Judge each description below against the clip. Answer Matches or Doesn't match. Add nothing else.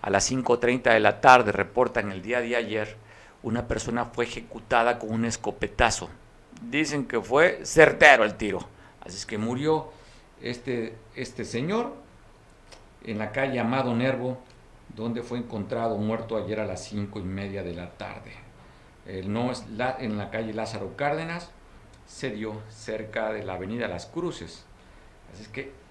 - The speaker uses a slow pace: Doesn't match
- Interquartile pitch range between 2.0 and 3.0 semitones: Matches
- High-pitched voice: Doesn't match